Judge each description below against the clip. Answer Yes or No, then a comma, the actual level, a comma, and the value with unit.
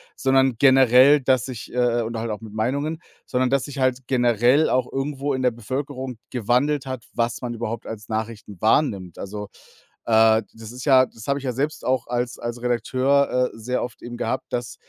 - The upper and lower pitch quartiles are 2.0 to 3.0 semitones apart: Yes, narrow, 2.6 semitones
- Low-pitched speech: Yes, low, 125 Hz